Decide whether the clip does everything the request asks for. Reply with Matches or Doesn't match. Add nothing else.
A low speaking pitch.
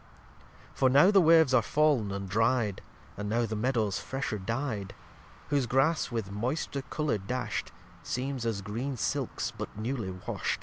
Matches